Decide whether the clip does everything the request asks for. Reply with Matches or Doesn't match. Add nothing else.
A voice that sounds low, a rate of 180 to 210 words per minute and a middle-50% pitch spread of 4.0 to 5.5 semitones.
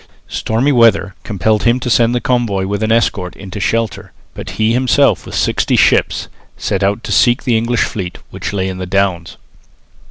Doesn't match